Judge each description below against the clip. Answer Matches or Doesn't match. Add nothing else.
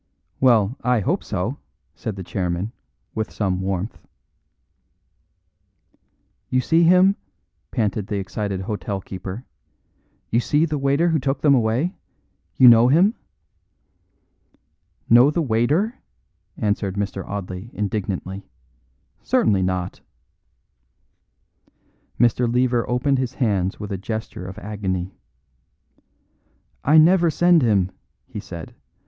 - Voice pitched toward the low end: Matches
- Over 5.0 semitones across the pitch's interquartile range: Matches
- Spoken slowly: Matches